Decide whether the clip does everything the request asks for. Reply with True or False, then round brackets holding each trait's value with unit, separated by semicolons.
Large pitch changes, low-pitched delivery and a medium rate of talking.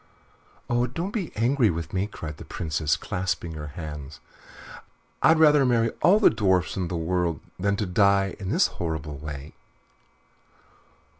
True (6.5 semitones; 90 Hz; 145 wpm)